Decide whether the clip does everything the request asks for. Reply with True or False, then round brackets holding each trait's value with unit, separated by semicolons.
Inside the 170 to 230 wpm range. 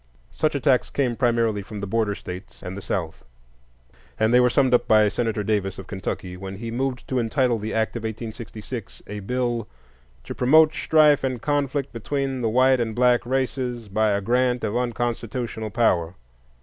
True (175 wpm)